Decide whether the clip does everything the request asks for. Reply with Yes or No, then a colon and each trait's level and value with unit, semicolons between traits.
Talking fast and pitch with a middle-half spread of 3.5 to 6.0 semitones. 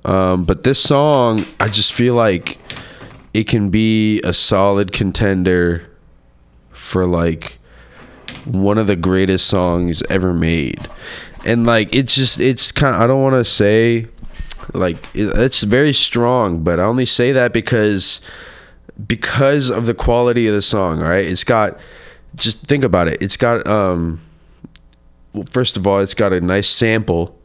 No: average, 155 wpm; average, 5.0 semitones